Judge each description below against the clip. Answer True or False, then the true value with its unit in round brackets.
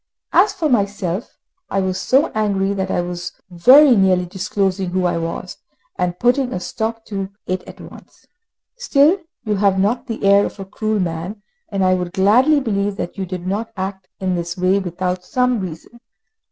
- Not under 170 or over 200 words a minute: True (180 wpm)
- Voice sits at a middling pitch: False (195 Hz)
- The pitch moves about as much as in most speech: True (3.4 semitones)